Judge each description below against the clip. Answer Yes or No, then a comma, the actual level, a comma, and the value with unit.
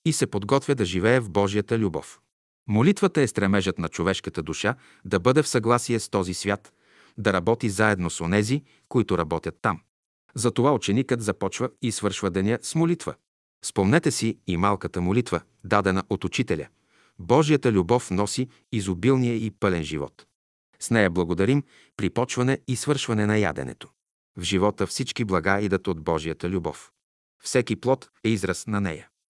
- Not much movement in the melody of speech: No, average, 4.5 semitones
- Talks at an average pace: Yes, average, 155 wpm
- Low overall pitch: Yes, low, 105 Hz